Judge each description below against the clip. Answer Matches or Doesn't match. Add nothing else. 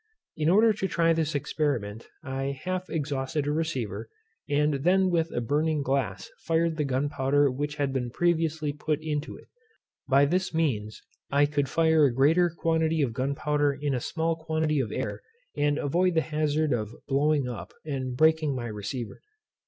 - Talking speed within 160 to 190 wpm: Matches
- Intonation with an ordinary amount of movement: Matches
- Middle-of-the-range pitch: Matches